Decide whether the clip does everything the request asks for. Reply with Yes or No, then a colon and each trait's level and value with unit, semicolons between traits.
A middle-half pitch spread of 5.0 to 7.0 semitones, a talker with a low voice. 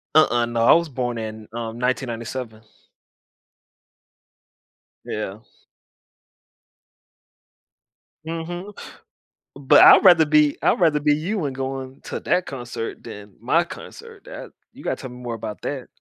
Yes: wide, 5.4 semitones; low, 130 Hz